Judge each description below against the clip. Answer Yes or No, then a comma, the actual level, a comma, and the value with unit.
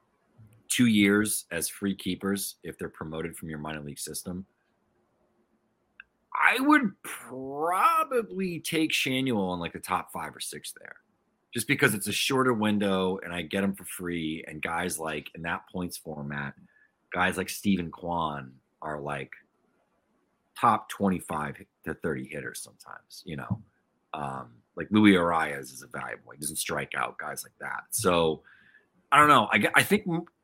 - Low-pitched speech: Yes, very low, 95 Hz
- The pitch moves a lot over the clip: Yes, wide, 5.9 semitones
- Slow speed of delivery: No, average, 160 wpm